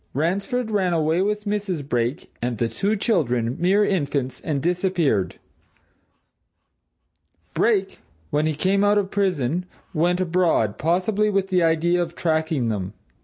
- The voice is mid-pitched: Yes, medium, 175 Hz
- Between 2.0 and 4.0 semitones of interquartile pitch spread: No, average, 5.2 semitones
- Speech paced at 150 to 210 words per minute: No, slow, 135 wpm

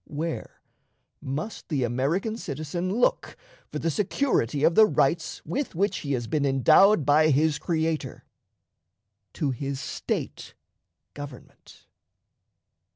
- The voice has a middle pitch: Yes, medium, 155 Hz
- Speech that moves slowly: Yes, slow, 115 wpm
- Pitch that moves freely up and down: No, average, 4.2 semitones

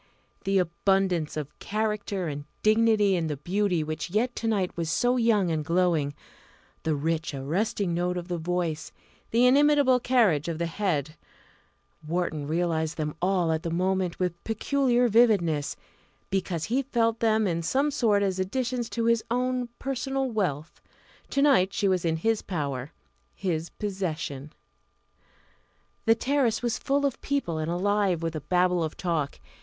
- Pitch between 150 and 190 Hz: Yes, medium, 185 Hz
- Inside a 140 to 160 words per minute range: Yes, average, 155 wpm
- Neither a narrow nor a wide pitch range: No, wide, 5.7 semitones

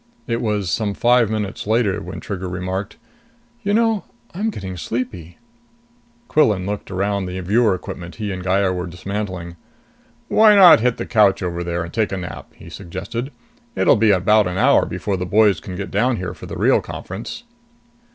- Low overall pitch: Yes, low, 100 Hz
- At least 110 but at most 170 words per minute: No, average, 180 wpm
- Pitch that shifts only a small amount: No, average, 3.5 semitones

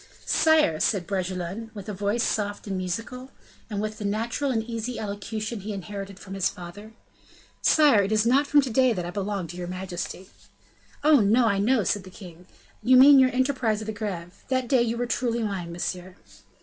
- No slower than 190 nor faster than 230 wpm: Yes, average, 195 wpm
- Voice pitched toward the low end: No, high, 210 Hz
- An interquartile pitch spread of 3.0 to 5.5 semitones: Yes, average, 4.0 semitones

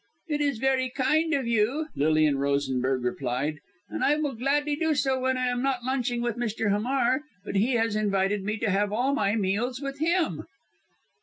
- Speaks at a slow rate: No, average, 185 wpm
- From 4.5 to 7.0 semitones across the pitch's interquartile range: Yes, average, 5.3 semitones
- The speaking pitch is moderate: No, high, 240 Hz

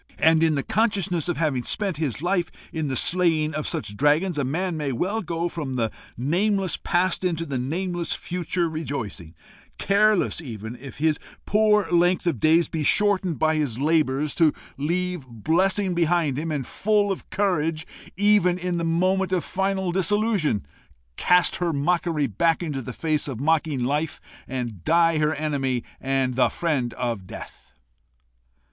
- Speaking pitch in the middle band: Yes, medium, 160 Hz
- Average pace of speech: Yes, average, 160 wpm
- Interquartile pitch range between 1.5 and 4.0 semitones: No, average, 4.4 semitones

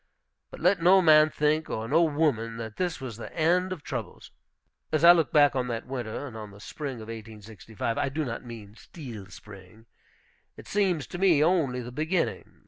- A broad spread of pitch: Yes, wide, 6.2 semitones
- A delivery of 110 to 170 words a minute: No, average, 200 wpm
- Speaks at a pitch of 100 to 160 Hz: Yes, low, 135 Hz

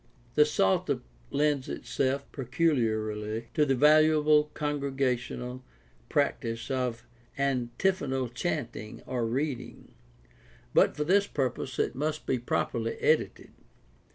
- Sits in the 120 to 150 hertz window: Yes, low, 135 Hz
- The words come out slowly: Yes, slow, 100 wpm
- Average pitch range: Yes, average, 3.8 semitones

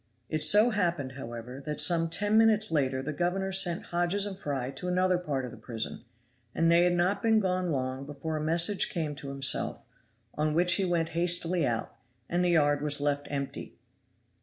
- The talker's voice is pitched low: No, medium, 165 Hz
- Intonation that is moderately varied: Yes, average, 4.2 semitones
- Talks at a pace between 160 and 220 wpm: Yes, average, 190 wpm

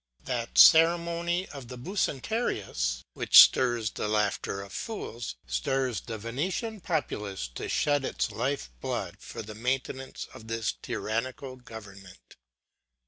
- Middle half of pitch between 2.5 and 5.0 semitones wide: No, wide, 5.4 semitones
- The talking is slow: Yes, slow, 125 wpm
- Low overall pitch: Yes, low, 125 Hz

